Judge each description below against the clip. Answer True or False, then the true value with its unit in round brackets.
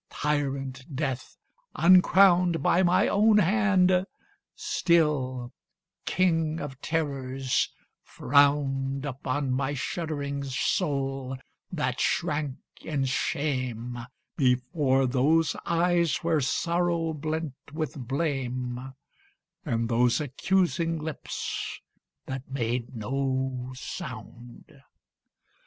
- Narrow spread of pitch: False (4.1 semitones)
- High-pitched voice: False (140 Hz)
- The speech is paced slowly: True (85 wpm)